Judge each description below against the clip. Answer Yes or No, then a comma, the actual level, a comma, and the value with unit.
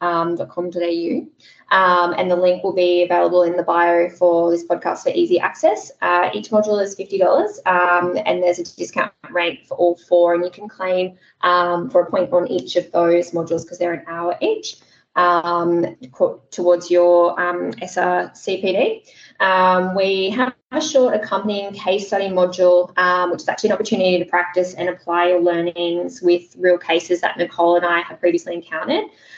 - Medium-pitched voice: Yes, medium, 180 Hz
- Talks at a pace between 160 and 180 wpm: Yes, average, 175 wpm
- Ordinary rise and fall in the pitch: No, narrow, 1.7 semitones